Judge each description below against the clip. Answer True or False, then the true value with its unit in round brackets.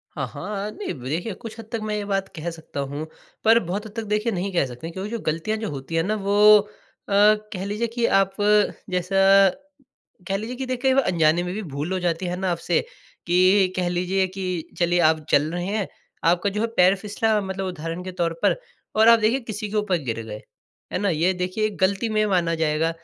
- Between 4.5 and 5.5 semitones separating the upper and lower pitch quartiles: False (3.6 semitones)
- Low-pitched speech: False (190 Hz)